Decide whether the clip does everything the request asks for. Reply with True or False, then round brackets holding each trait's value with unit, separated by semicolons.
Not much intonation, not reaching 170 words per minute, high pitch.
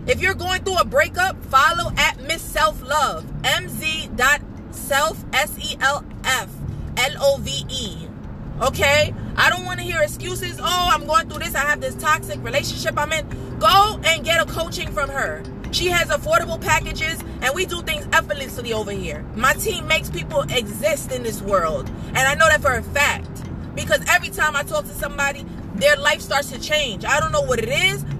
False (2.1 semitones; 180 wpm; 310 Hz)